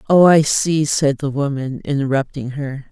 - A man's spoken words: No, female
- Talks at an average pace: Yes, average, 165 wpm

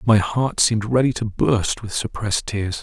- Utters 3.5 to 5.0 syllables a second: Yes, 4.8 syllables/s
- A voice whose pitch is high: No, low, 110 Hz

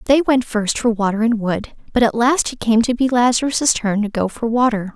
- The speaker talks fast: Yes, fast, 240 wpm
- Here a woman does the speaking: Yes, female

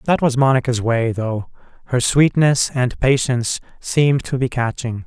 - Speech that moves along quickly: No, average, 155 wpm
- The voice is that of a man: Yes, male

